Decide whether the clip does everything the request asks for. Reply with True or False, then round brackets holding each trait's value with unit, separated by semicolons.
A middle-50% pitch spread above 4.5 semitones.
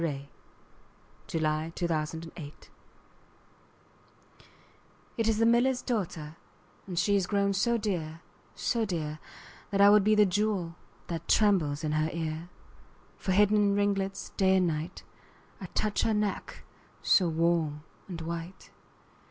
False (4.2 semitones)